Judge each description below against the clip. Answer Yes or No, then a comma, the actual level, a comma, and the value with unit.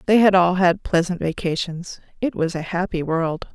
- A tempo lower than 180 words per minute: No, average, 185 wpm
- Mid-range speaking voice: Yes, medium, 175 Hz